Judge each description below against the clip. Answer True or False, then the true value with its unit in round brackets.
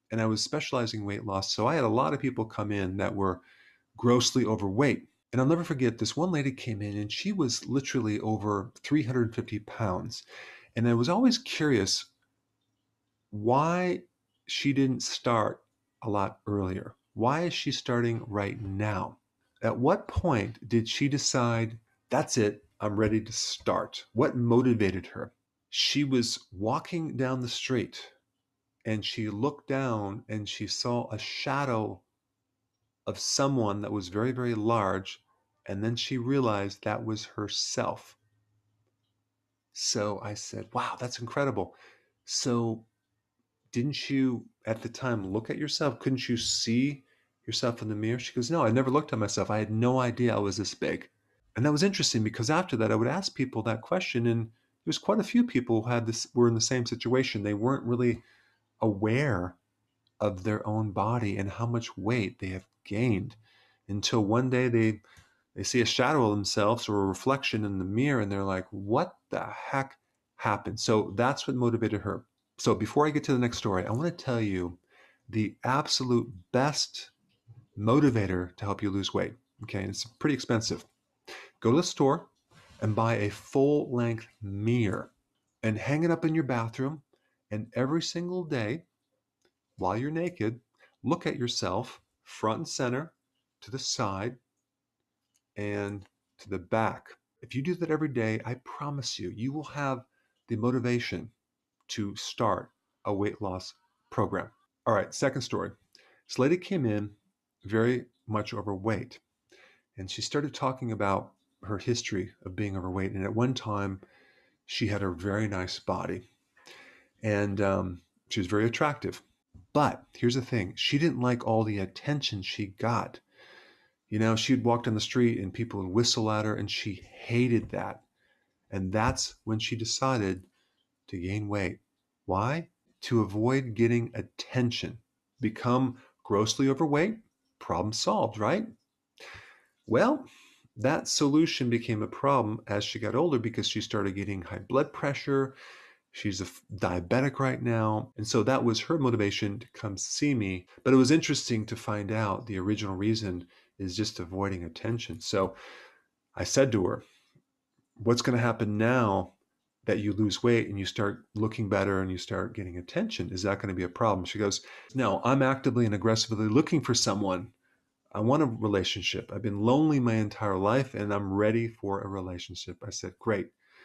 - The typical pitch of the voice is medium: False (115 Hz)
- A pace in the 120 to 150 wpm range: False (165 wpm)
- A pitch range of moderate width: True (3.7 semitones)